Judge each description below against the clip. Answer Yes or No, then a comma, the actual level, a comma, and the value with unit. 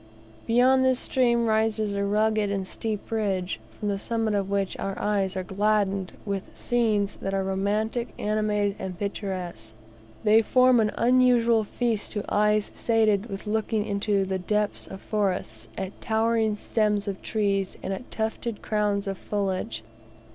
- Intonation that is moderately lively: No, narrow, 2.1 semitones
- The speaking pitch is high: Yes, high, 210 Hz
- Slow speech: No, average, 155 wpm